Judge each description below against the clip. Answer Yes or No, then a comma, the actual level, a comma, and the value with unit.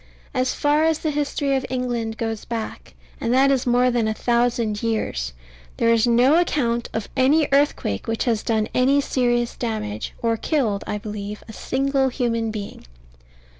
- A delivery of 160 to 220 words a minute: Yes, average, 170 wpm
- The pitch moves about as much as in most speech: Yes, average, 3.2 semitones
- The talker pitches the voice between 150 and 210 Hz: No, high, 240 Hz